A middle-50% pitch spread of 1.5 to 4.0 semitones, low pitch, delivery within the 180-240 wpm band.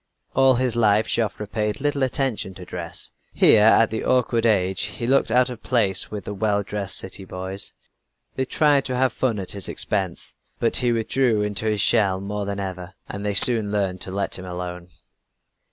Yes: average, 3.7 semitones; low, 105 Hz; average, 190 wpm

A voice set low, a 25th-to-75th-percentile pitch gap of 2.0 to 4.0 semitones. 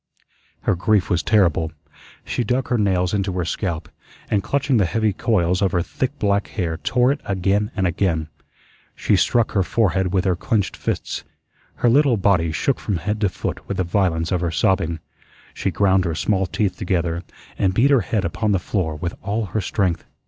Yes: very low, 95 Hz; average, 3.6 semitones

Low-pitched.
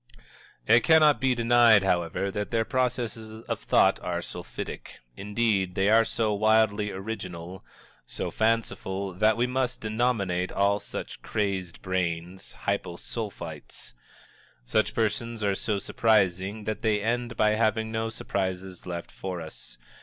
Yes: low, 105 Hz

